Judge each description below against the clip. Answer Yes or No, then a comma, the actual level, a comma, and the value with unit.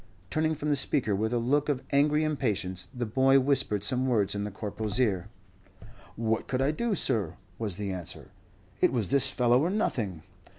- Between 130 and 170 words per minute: No, average, 185 wpm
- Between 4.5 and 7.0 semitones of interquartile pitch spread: Yes, average, 5.2 semitones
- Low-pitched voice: Yes, low, 125 Hz